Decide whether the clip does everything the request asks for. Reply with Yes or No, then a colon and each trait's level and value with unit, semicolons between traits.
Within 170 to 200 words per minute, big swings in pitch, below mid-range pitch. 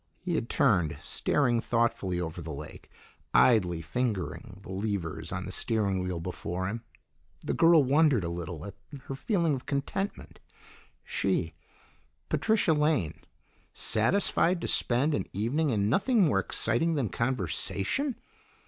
No: slow, 135 wpm; wide, 8.4 semitones; low, 115 Hz